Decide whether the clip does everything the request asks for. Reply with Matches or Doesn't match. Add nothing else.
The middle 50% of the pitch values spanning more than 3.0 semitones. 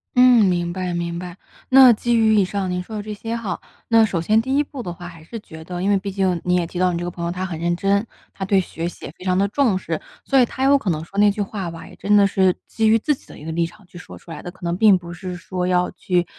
Matches